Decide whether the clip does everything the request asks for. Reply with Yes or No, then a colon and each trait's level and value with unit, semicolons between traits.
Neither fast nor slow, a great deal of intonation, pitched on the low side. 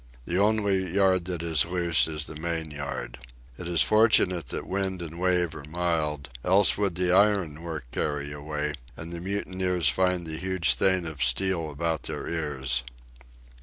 No: average, 165 wpm; average, 3.3 semitones; very low, 85 Hz